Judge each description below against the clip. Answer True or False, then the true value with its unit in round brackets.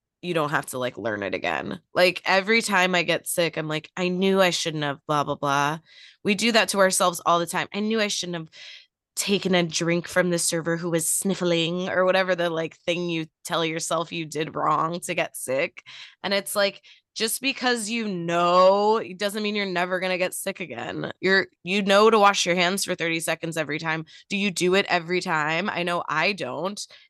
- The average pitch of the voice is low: False (175 Hz)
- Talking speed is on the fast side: True (220 wpm)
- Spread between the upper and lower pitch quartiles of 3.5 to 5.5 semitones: False (2.9 semitones)